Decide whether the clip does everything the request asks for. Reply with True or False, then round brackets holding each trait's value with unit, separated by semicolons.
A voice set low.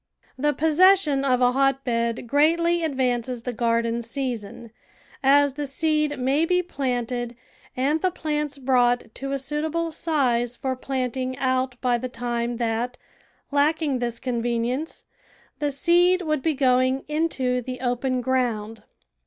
False (260 Hz)